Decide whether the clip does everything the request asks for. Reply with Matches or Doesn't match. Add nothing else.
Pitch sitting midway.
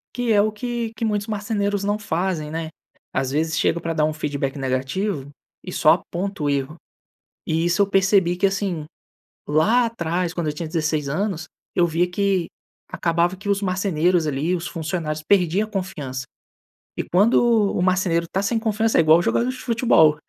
Matches